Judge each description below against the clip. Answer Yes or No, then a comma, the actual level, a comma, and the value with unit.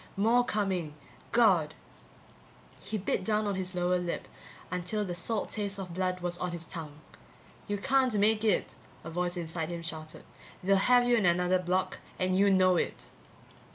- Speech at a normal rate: Yes, average, 170 wpm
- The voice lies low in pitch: No, medium, 185 Hz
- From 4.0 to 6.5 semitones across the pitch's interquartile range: No, average, 2.9 semitones